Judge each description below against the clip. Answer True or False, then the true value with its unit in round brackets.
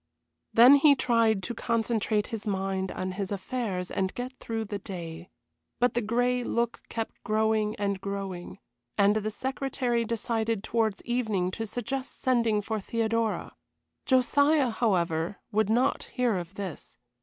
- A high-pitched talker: True (220 Hz)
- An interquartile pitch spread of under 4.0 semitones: True (3.3 semitones)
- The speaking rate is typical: True (145 wpm)